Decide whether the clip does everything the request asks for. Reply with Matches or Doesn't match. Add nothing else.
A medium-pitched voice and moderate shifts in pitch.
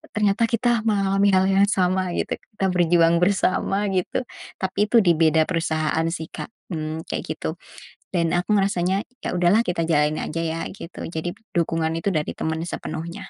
Matches